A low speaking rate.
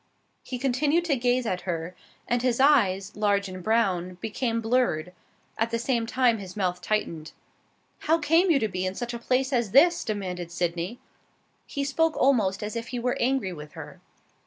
No: average, 185 wpm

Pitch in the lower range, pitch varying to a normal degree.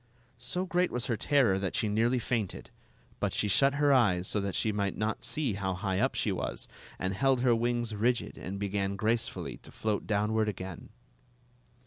Yes: low, 110 Hz; average, 3.8 semitones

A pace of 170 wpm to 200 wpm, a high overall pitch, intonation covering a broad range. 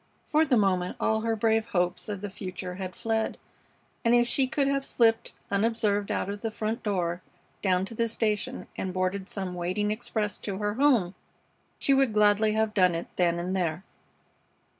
No: average, 185 wpm; high, 210 Hz; average, 3.4 semitones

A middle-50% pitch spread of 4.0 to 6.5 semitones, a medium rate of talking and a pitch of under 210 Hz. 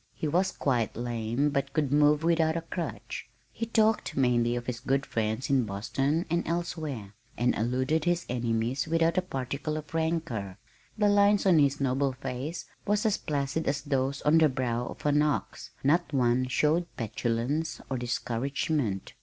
Yes: average, 4.8 semitones; average, 170 wpm; medium, 140 Hz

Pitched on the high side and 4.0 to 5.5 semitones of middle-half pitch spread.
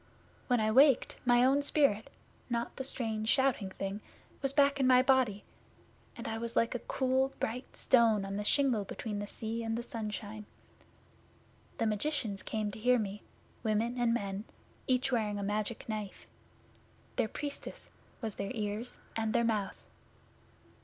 No: high, 230 Hz; average, 3.3 semitones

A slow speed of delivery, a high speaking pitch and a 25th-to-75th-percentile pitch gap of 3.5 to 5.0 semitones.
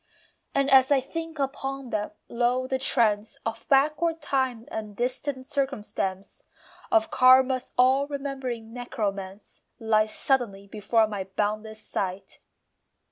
Yes: slow, 120 wpm; very high, 250 Hz; average, 4.1 semitones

